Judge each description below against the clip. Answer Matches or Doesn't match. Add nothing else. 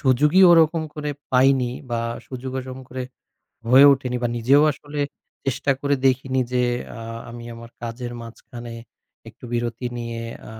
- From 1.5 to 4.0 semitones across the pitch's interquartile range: Matches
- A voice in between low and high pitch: Doesn't match